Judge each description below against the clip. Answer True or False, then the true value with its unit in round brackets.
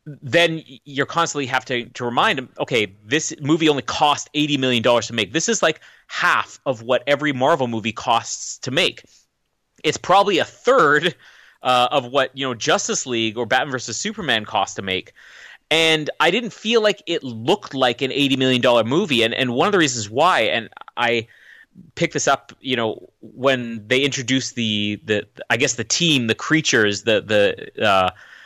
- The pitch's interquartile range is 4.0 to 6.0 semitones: True (4.6 semitones)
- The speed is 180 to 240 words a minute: True (190 wpm)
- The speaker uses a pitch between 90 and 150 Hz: True (135 Hz)